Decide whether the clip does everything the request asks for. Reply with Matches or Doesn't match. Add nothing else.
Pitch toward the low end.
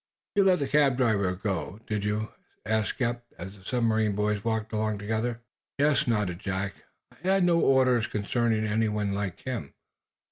Matches